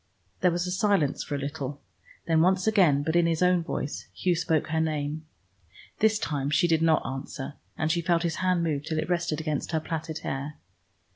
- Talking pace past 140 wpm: Yes, average, 200 wpm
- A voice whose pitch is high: No, medium, 160 Hz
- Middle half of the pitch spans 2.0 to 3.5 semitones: Yes, average, 2.7 semitones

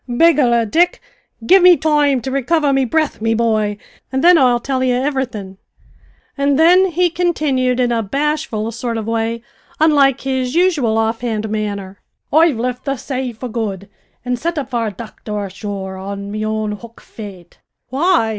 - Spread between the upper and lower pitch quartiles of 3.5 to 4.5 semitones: No, average, 5.1 semitones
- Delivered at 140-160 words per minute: No, average, 170 wpm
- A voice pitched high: Yes, high, 245 Hz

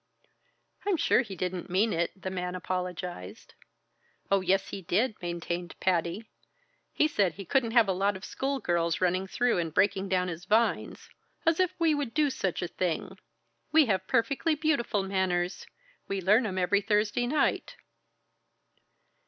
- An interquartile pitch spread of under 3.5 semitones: No, average, 4.6 semitones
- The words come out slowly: No, average, 160 wpm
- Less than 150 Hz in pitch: No, high, 195 Hz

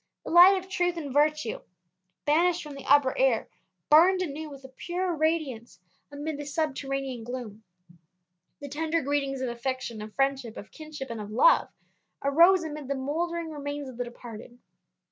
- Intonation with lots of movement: No, average, 3.6 semitones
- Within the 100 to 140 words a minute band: No, average, 165 wpm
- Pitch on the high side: Yes, very high, 285 Hz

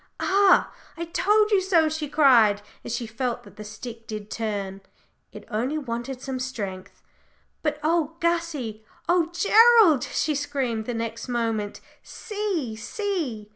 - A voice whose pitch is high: Yes, very high, 260 Hz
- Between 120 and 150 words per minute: Yes, average, 140 wpm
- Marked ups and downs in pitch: Yes, wide, 7.1 semitones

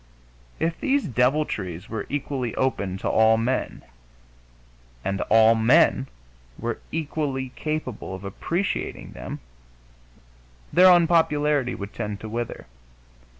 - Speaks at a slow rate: Yes, slow, 105 wpm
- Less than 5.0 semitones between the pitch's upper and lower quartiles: No, wide, 5.6 semitones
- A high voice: No, low, 125 Hz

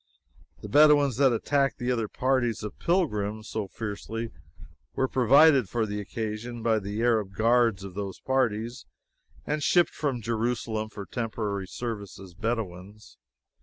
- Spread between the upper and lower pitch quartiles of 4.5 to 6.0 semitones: No, average, 3.3 semitones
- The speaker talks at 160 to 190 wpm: No, average, 140 wpm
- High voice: No, low, 115 Hz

